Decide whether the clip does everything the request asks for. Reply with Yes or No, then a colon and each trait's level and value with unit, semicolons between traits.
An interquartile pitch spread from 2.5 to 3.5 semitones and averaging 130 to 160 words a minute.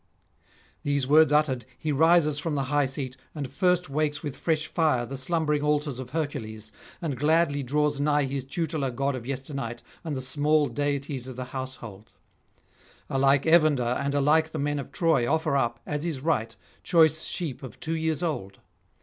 No: average, 3.0 semitones; average, 175 wpm